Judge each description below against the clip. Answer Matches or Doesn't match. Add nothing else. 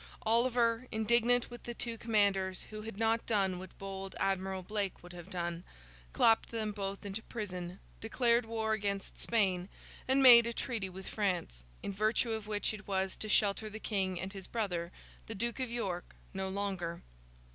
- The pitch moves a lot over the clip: Doesn't match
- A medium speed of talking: Matches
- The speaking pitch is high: Matches